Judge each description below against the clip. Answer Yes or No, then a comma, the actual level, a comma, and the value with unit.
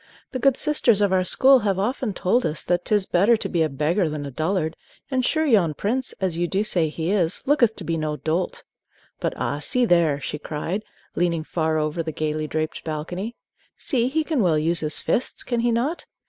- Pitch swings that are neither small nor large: No, wide, 6.8 semitones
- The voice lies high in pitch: No, medium, 180 Hz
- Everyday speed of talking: No, fast, 215 wpm